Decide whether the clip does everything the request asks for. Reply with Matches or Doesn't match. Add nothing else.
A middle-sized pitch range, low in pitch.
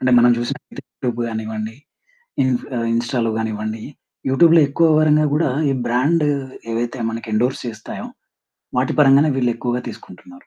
Matches